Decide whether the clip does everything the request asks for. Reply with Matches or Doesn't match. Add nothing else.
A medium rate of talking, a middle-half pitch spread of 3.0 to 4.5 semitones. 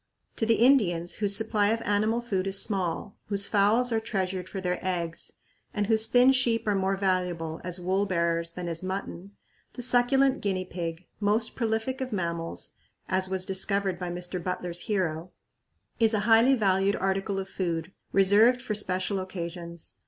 Matches